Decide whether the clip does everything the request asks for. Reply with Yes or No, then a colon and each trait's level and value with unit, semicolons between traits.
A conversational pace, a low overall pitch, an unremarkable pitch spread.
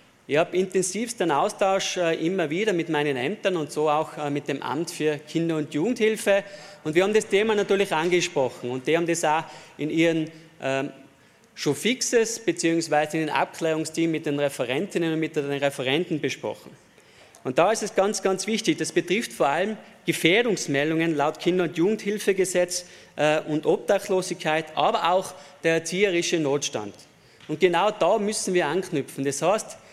No: average, 160 wpm; medium, 165 Hz; average, 4.2 semitones